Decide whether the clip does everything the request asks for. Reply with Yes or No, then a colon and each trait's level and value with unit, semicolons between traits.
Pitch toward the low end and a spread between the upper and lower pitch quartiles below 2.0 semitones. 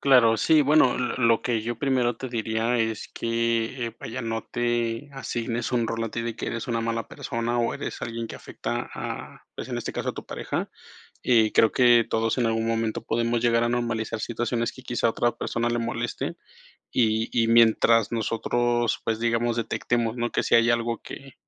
Yes: low, 115 Hz; narrow, 0.9 semitones